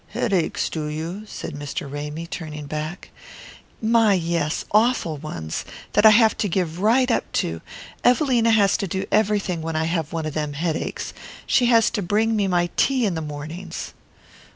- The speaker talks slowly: No, average, 175 wpm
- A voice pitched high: No, medium, 175 Hz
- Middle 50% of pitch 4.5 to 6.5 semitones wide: Yes, wide, 5.6 semitones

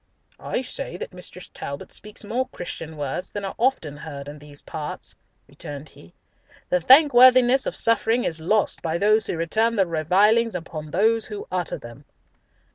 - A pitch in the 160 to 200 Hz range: Yes, high, 190 Hz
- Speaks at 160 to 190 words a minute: Yes, average, 165 wpm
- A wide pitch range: Yes, wide, 6.5 semitones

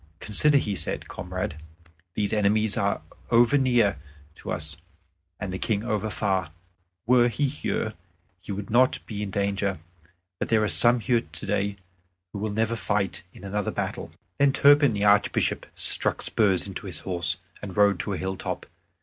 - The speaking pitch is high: No, low, 105 Hz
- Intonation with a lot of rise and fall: No, average, 2.8 semitones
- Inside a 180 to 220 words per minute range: No, average, 165 wpm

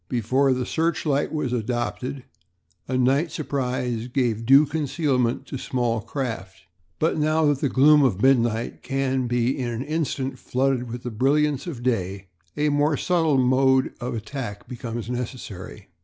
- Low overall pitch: Yes, low, 130 Hz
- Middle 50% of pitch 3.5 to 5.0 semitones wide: No, average, 3.0 semitones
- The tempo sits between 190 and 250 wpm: No, average, 150 wpm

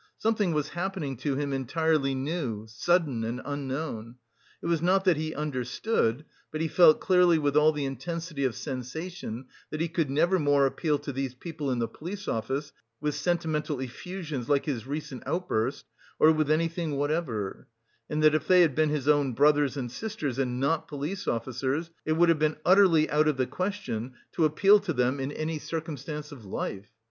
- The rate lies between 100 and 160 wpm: No, average, 185 wpm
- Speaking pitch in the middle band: Yes, medium, 150 Hz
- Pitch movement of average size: Yes, average, 3.8 semitones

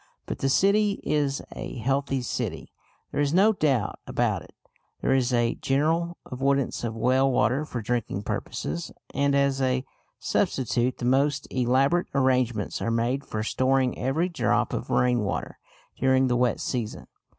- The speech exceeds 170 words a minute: No, average, 155 wpm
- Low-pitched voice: Yes, low, 130 Hz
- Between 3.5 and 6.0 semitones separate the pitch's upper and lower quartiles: No, narrow, 2.4 semitones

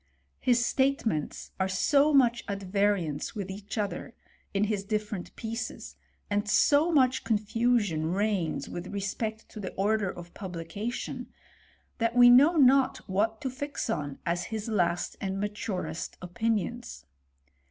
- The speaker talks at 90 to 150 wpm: Yes, slow, 135 wpm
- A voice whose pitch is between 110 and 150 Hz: No, high, 210 Hz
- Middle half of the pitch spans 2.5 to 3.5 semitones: No, average, 4.1 semitones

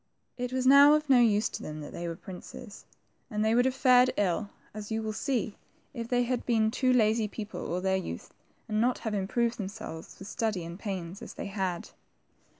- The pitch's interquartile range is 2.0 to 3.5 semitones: No, average, 4.3 semitones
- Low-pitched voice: No, high, 220 Hz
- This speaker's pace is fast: Yes, fast, 210 wpm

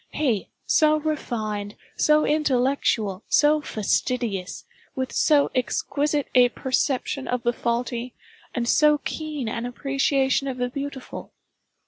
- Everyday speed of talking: No, slow, 115 wpm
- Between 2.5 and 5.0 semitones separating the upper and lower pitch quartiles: Yes, average, 3.6 semitones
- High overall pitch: Yes, very high, 260 Hz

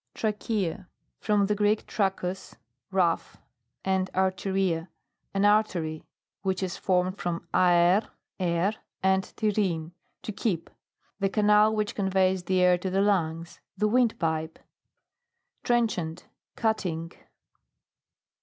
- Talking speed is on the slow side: Yes, slow, 105 wpm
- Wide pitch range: No, average, 3.0 semitones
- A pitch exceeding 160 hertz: Yes, high, 190 Hz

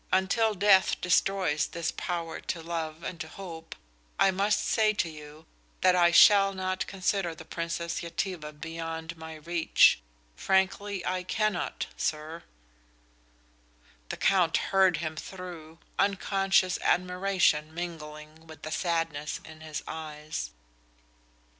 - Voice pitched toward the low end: No, medium, 170 Hz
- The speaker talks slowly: Yes, slow, 120 wpm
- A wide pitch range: No, average, 3.0 semitones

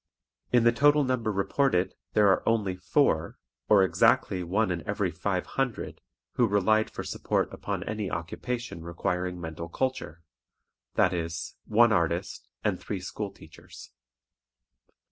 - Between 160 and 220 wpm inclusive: No, slow, 135 wpm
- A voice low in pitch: Yes, low, 100 Hz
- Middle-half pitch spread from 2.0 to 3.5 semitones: No, average, 4.3 semitones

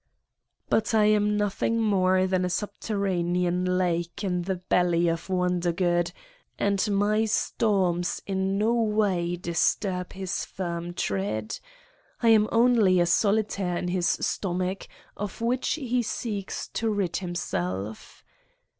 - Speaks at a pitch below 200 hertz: Yes, medium, 185 Hz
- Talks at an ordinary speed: No, slow, 125 wpm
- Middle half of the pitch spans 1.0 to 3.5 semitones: Yes, average, 3.1 semitones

